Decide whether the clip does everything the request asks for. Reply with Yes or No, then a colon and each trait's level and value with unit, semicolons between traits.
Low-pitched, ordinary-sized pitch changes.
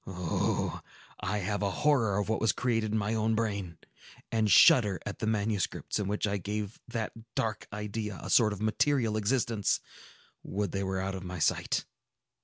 No: low, 105 Hz; narrow, 2.1 semitones